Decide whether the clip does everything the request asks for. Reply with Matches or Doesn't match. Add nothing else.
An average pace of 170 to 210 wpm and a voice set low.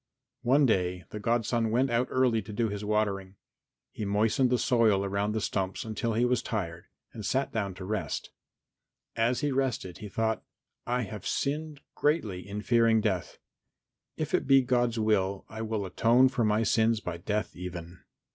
Matches